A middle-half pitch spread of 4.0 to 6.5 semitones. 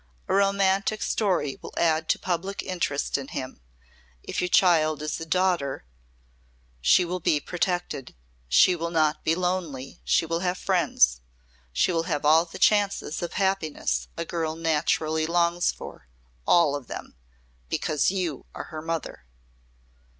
No: average, 2.9 semitones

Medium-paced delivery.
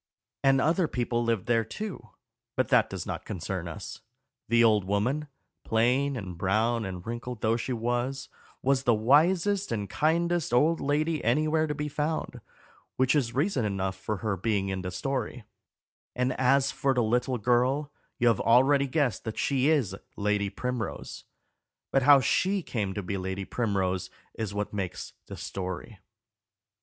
Yes: average, 160 wpm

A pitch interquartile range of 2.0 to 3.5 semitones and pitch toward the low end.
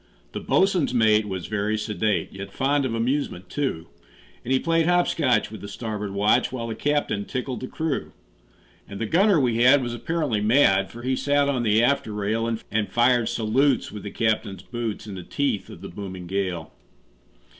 No: average, 4.7 semitones; low, 115 Hz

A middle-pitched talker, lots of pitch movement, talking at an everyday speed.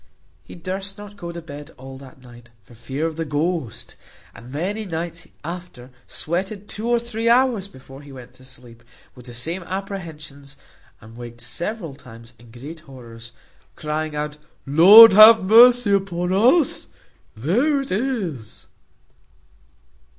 Yes: medium, 165 Hz; wide, 7.1 semitones; average, 150 wpm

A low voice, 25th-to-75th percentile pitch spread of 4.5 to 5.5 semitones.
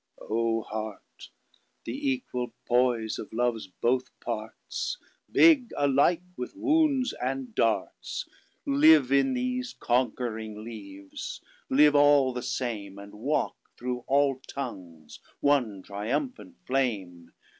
Yes: low, 125 Hz; average, 4.8 semitones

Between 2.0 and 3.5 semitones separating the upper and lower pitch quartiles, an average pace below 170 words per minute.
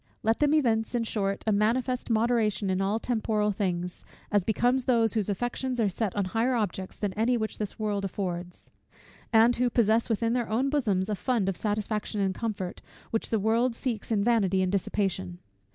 No: average, 3.1 semitones; average, 185 wpm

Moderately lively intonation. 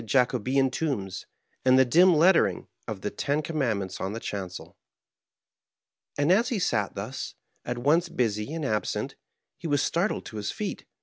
No: wide, 7.0 semitones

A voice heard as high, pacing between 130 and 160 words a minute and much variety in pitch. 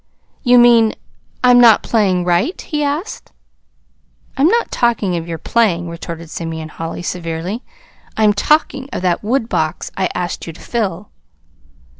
Yes: high, 200 Hz; average, 140 wpm; wide, 6.2 semitones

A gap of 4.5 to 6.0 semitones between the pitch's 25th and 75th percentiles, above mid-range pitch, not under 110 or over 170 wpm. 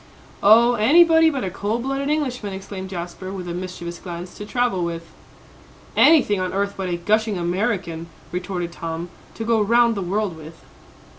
Yes: average, 4.8 semitones; high, 195 Hz; average, 165 wpm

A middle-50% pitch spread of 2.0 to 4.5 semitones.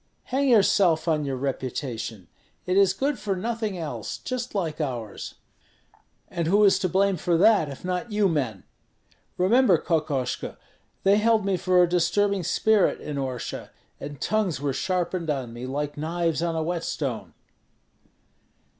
No: wide, 5.4 semitones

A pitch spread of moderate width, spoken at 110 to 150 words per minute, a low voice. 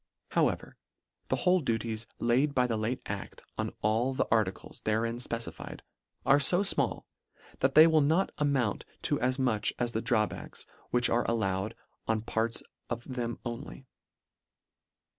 Yes: average, 3.2 semitones; average, 145 wpm; low, 120 Hz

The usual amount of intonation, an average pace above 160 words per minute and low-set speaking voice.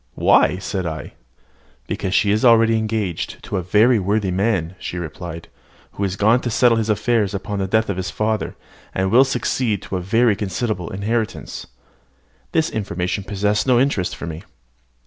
Yes: average, 3.3 semitones; average, 170 wpm; low, 105 Hz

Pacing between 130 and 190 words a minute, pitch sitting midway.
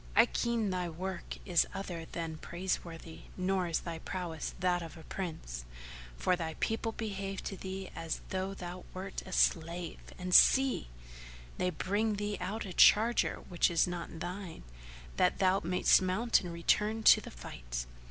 Yes: average, 160 wpm; medium, 180 Hz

